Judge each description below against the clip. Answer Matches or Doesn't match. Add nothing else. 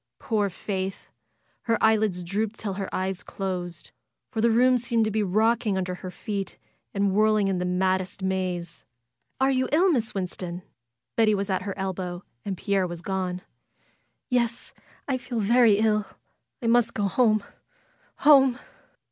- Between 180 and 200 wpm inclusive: Doesn't match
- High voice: Matches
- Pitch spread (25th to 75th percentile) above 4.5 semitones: Doesn't match